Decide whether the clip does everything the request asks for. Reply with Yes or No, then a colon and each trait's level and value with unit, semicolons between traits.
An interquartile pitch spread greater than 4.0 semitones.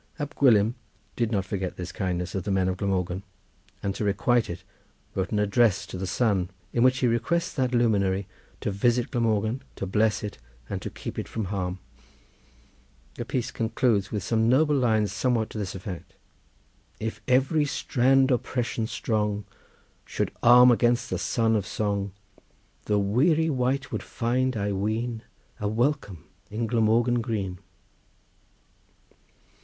No: average, 3.6 semitones